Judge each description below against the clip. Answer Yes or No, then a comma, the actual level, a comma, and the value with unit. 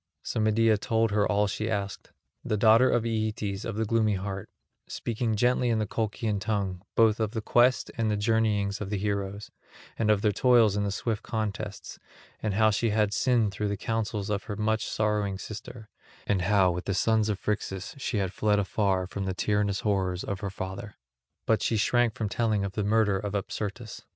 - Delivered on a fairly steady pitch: Yes, narrow, 1.8 semitones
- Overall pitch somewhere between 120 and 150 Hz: No, low, 105 Hz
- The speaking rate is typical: Yes, average, 195 wpm